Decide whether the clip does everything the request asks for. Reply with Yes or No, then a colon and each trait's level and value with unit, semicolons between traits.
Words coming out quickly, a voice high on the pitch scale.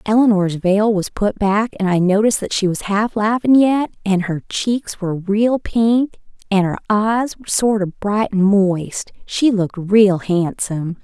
No: average, 170 wpm; high, 205 Hz